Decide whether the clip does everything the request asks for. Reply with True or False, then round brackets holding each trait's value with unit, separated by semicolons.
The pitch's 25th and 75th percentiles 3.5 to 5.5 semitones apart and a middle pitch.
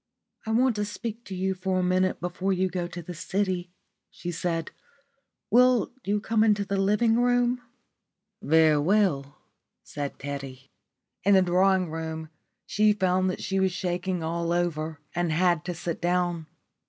False (3.0 semitones; 180 Hz)